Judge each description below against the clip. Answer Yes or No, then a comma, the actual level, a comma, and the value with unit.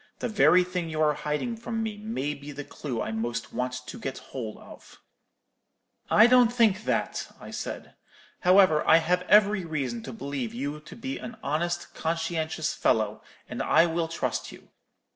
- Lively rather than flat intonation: Yes, wide, 6.7 semitones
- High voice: No, medium, 160 Hz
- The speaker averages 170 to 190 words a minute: Yes, average, 175 wpm